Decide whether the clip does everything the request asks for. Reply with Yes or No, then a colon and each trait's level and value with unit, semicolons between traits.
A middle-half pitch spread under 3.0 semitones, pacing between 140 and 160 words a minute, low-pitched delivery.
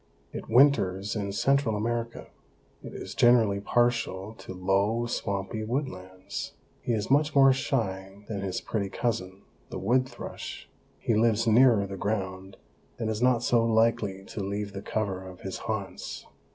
No: average, 3.4 semitones; average, 150 wpm; low, 105 Hz